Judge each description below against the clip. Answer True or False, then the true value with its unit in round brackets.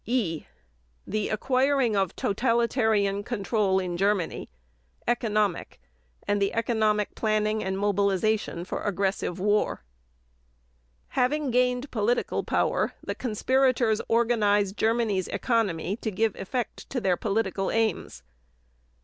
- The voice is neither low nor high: False (215 Hz)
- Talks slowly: True (105 wpm)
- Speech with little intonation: False (3.0 semitones)